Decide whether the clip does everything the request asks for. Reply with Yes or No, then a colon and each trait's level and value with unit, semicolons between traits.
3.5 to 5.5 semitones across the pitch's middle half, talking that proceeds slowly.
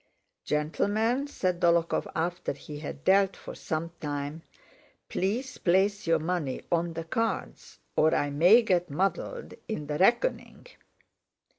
Yes: average, 4.4 semitones; slow, 130 wpm